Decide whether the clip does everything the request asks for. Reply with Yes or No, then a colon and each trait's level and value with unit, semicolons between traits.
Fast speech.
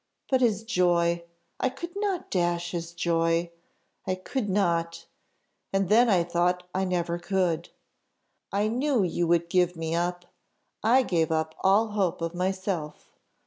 No: average, 145 wpm